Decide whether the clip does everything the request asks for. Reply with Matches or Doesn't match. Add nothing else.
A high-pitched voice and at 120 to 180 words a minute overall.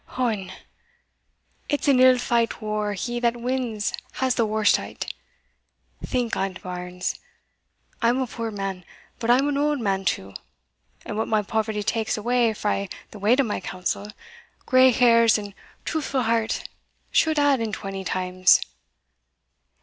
Matches